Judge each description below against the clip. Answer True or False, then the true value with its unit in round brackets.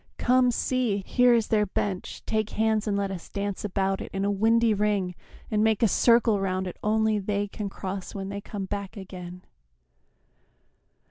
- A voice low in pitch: False (205 Hz)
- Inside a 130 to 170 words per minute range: False (180 wpm)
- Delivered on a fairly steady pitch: True (2.1 semitones)